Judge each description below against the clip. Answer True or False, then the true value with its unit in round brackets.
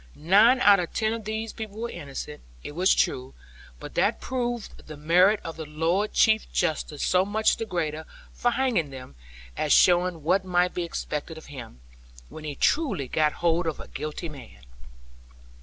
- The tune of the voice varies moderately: False (5.8 semitones)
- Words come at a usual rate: True (175 wpm)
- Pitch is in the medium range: True (175 Hz)